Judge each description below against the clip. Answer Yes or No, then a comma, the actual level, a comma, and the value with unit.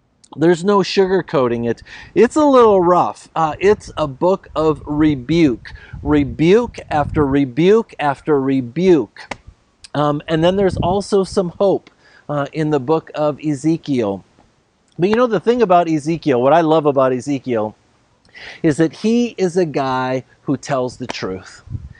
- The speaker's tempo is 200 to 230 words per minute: No, average, 145 wpm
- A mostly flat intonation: No, average, 5.3 semitones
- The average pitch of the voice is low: No, medium, 155 Hz